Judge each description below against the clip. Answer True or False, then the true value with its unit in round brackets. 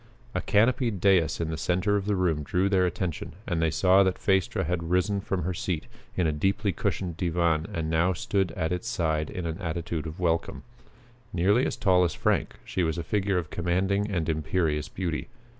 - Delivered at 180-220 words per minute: True (200 wpm)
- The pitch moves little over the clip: False (3.0 semitones)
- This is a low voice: True (90 Hz)